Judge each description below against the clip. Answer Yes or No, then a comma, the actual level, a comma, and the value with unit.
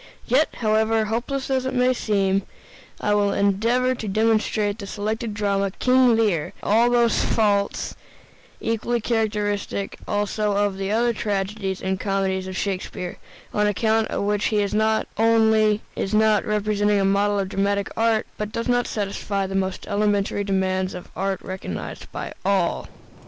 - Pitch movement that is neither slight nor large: No, narrow, 2.1 semitones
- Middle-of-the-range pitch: No, high, 210 Hz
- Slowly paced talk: No, average, 155 wpm